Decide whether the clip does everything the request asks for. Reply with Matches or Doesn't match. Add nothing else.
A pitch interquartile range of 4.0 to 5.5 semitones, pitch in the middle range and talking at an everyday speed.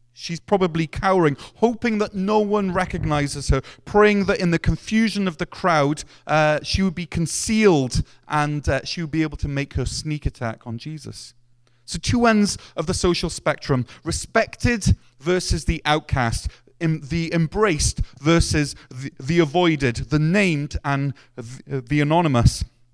Matches